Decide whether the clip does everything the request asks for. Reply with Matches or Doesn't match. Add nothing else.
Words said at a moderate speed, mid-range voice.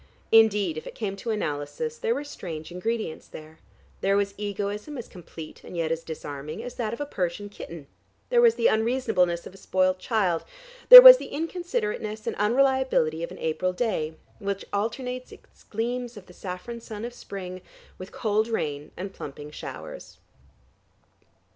Doesn't match